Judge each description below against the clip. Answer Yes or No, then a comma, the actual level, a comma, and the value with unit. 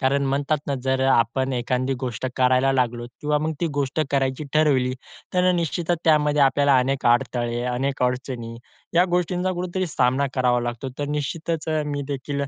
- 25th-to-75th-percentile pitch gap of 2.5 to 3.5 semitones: Yes, average, 3.0 semitones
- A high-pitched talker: No, low, 135 Hz